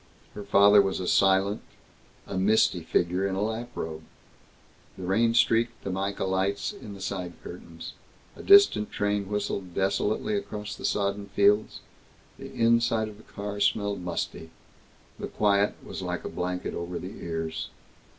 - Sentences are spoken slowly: No, average, 150 wpm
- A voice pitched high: No, low, 100 Hz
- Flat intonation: Yes, narrow, 2.0 semitones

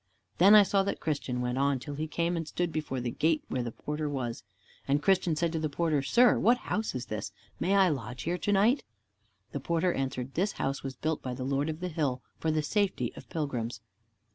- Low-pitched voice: No, medium, 155 Hz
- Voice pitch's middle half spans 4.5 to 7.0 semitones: Yes, average, 4.8 semitones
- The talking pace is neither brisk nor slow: No, fast, 225 wpm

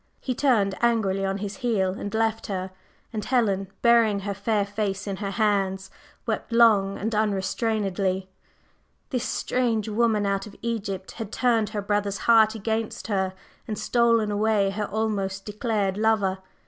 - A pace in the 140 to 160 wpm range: Yes, average, 150 wpm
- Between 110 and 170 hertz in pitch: No, high, 210 Hz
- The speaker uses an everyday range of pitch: No, narrow, 2.3 semitones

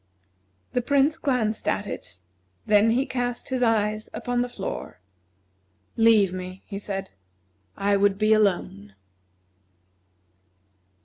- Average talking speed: No, slow, 120 wpm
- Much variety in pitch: No, average, 3.7 semitones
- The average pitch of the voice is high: Yes, high, 215 Hz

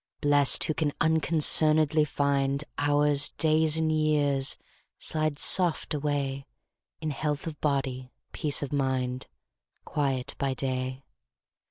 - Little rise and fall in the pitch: Yes, narrow, 2.2 semitones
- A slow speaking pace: Yes, slow, 115 wpm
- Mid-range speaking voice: Yes, medium, 145 Hz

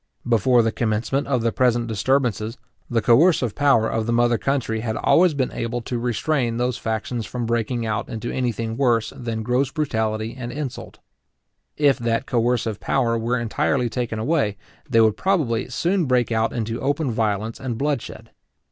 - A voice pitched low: Yes, low, 120 Hz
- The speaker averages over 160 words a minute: Yes, average, 170 wpm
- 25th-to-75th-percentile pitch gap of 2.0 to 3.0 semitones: Yes, narrow, 2.4 semitones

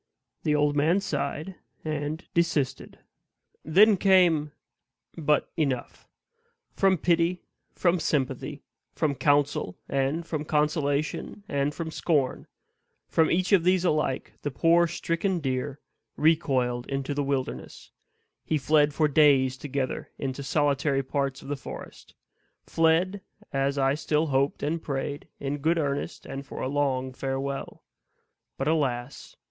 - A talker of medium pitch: Yes, medium, 145 Hz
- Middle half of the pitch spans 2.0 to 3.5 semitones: Yes, average, 3.0 semitones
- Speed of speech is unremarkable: No, slow, 130 wpm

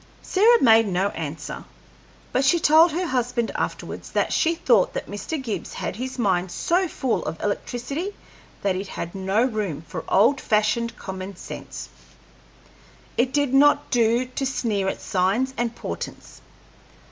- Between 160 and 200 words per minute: No, average, 150 wpm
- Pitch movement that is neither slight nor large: No, wide, 5.7 semitones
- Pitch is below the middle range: No, high, 230 Hz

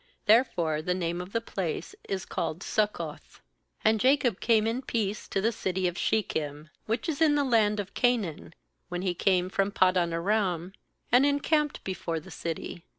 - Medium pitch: No, high, 195 Hz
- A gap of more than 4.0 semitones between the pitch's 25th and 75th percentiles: Yes, average, 4.6 semitones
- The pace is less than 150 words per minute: No, average, 170 wpm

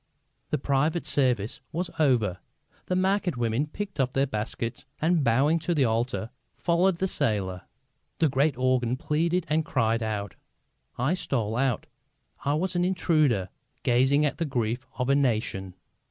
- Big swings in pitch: Yes, wide, 5.7 semitones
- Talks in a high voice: No, low, 135 Hz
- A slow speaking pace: No, average, 155 wpm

